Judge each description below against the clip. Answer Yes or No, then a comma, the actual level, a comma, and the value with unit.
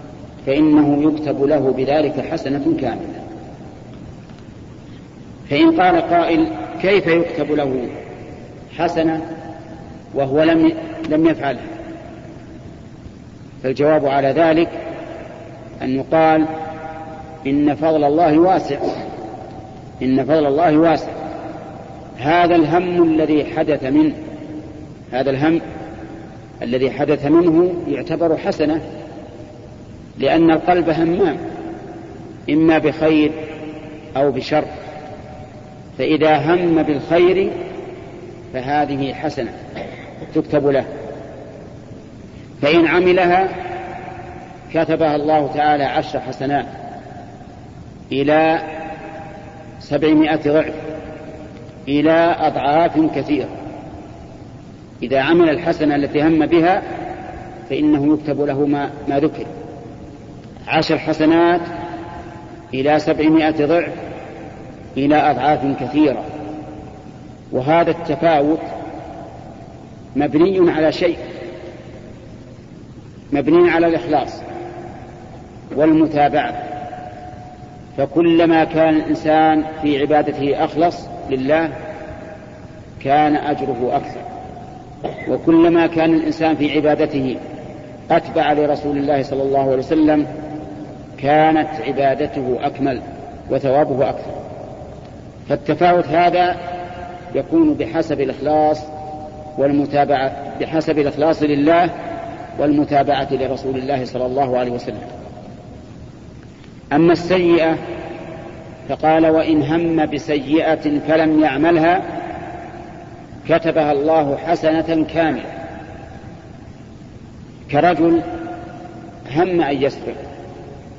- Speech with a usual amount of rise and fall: No, narrow, 2.2 semitones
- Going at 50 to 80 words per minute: Yes, average, 75 wpm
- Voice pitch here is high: No, medium, 155 Hz